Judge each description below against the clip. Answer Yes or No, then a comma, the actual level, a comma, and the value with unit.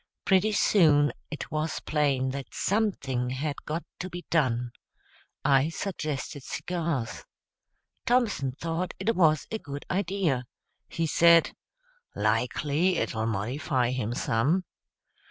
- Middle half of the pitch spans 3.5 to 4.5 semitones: No, average, 5.3 semitones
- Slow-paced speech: Yes, slow, 115 wpm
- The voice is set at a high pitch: No, medium, 150 Hz